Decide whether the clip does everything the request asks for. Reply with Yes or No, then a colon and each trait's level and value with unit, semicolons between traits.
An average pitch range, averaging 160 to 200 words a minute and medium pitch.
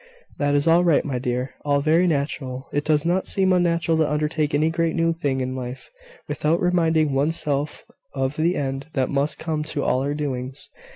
Yes: average, 3.1 semitones; average, 195 wpm; medium, 150 Hz